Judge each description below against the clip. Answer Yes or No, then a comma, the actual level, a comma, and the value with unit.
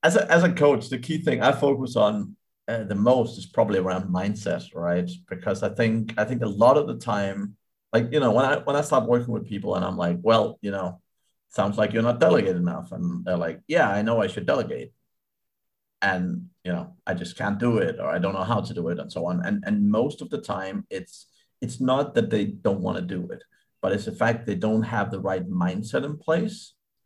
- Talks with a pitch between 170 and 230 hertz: No, low, 120 Hz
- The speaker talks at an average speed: No, fast, 240 wpm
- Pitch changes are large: Yes, wide, 7.9 semitones